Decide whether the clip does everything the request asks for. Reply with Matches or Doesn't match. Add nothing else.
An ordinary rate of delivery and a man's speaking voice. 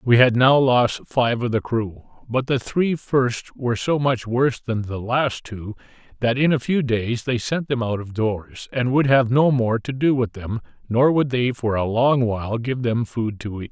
Doesn't match